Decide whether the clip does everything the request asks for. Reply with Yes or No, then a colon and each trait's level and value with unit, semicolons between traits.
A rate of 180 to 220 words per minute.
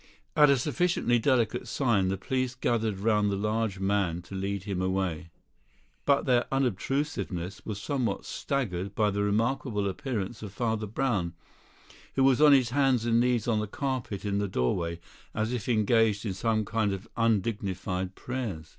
No: average, 165 wpm